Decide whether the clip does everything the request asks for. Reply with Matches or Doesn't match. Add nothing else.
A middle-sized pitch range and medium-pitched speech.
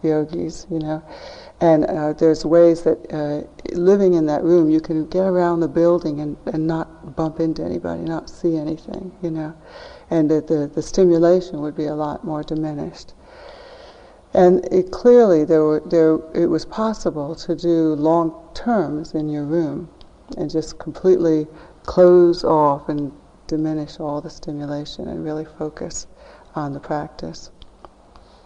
Doesn't match